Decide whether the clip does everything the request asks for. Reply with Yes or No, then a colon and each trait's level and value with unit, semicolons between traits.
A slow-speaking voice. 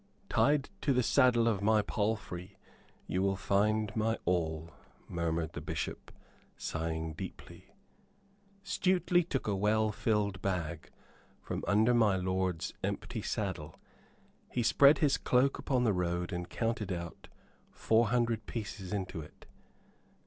Yes: slow, 130 wpm